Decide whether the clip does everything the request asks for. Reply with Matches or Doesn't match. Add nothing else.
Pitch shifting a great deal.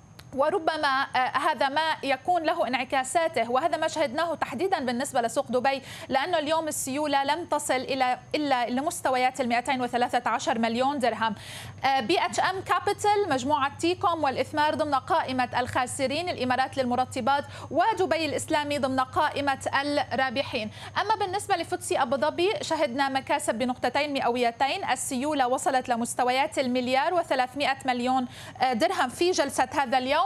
Doesn't match